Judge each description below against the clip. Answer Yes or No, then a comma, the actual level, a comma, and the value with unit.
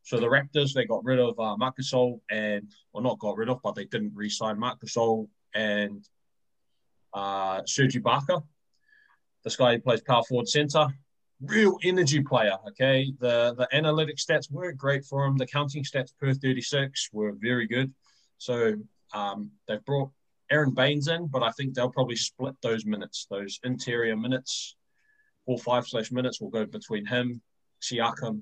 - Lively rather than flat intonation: No, average, 3.9 semitones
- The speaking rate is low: No, average, 170 wpm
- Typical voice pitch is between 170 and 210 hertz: No, low, 125 Hz